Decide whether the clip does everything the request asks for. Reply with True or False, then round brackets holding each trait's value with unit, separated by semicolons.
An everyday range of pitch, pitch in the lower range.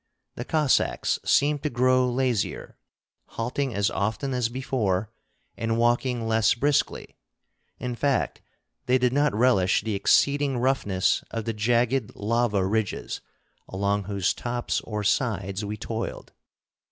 True (3.5 semitones; 115 Hz)